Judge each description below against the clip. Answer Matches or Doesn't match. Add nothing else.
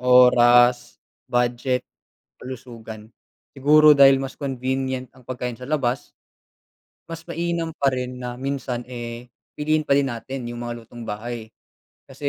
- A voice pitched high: Doesn't match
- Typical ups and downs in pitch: Doesn't match